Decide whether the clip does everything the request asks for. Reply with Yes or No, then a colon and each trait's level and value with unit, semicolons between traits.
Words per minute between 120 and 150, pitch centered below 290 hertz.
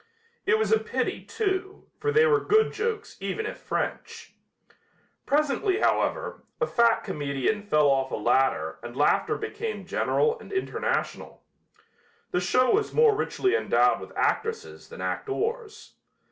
No: average, 140 wpm; very high, 405 Hz